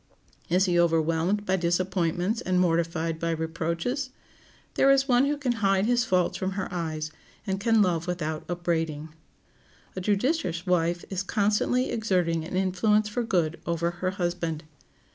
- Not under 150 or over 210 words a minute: Yes, average, 155 wpm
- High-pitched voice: No, medium, 180 Hz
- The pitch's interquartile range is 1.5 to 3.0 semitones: No, average, 3.8 semitones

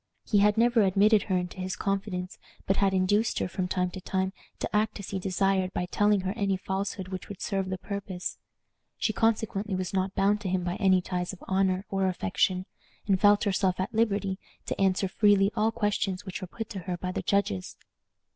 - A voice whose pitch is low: No, high, 195 Hz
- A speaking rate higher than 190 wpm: Yes, fast, 205 wpm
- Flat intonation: Yes, narrow, 1.7 semitones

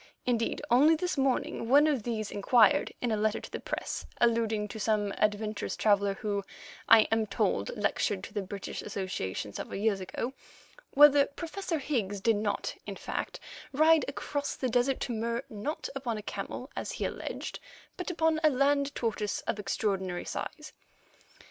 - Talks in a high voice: Yes, high, 230 Hz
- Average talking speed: Yes, average, 165 wpm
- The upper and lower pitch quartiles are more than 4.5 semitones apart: Yes, average, 5.2 semitones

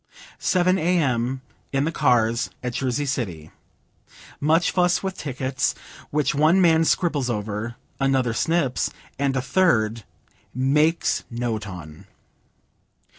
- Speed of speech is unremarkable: No, slow, 115 wpm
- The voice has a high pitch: No, low, 135 Hz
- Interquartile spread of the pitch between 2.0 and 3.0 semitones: No, wide, 5.4 semitones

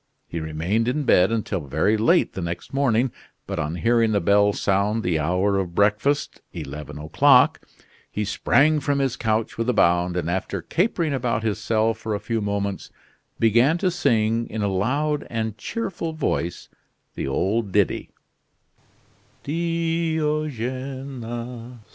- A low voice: Yes, low, 110 Hz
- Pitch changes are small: No, wide, 5.5 semitones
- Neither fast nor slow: Yes, average, 145 wpm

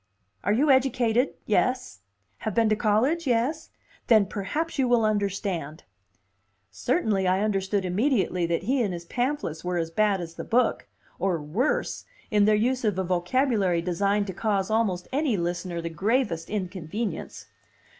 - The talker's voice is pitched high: Yes, high, 205 Hz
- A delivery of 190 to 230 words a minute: No, average, 155 wpm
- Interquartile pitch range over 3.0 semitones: Yes, average, 5.2 semitones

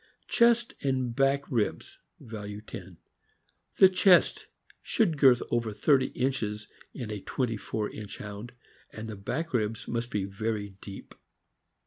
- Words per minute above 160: No, average, 140 wpm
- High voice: No, low, 115 Hz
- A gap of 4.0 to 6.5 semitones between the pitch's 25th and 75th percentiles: Yes, average, 4.5 semitones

